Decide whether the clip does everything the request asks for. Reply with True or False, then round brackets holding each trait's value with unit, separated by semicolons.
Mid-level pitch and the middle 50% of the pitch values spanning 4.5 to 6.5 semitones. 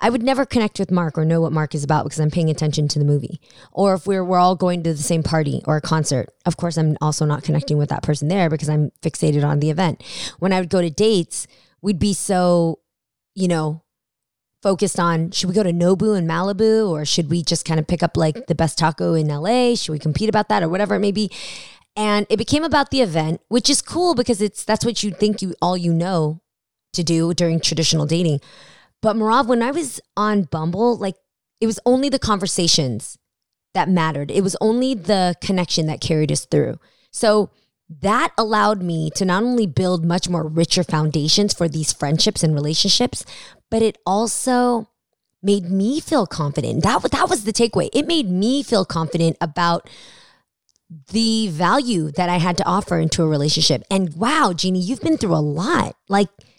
True (180 Hz; 4.9 semitones)